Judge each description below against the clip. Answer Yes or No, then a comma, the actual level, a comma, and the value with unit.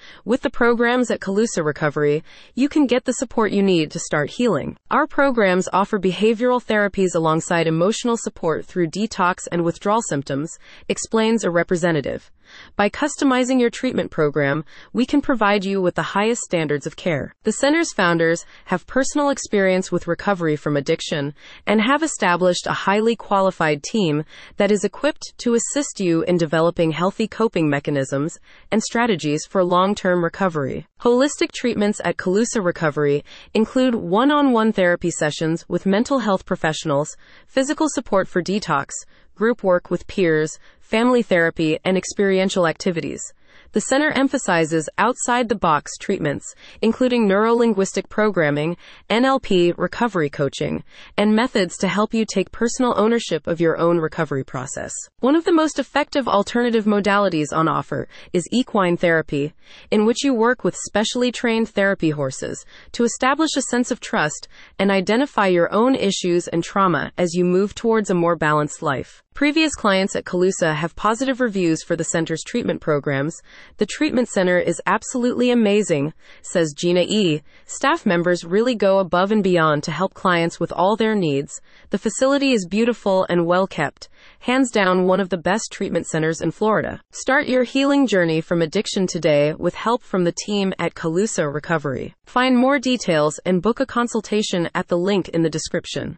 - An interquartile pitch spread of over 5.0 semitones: Yes, wide, 5.5 semitones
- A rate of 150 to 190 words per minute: Yes, average, 160 wpm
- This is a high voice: Yes, high, 195 Hz